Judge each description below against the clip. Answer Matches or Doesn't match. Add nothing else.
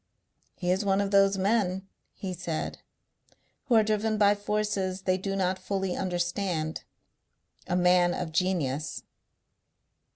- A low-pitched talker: Doesn't match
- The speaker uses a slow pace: Matches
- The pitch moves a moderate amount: Doesn't match